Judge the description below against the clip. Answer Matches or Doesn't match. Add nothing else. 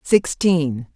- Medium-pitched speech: Matches